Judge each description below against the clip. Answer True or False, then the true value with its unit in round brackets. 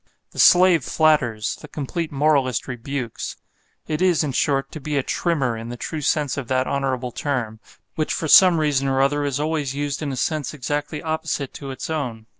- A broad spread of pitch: False (3.0 semitones)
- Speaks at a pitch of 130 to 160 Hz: True (140 Hz)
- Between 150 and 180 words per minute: False (195 wpm)